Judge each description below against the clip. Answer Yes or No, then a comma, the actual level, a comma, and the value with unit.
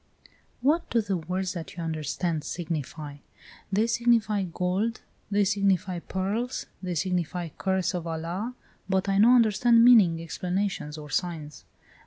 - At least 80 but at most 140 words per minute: Yes, slow, 135 wpm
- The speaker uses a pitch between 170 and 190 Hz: Yes, medium, 185 Hz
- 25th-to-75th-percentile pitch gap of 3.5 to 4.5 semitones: Yes, average, 4.1 semitones